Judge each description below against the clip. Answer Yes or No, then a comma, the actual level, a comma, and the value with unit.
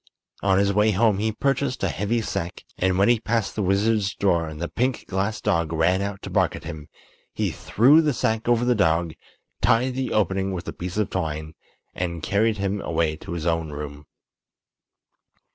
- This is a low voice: Yes, low, 100 Hz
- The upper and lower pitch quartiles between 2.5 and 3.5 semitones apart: No, average, 4.8 semitones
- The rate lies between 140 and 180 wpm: No, average, 195 wpm